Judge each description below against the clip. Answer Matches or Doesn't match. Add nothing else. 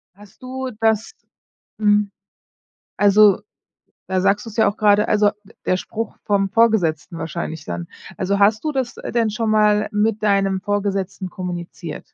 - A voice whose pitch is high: Matches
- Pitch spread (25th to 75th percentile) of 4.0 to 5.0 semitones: Doesn't match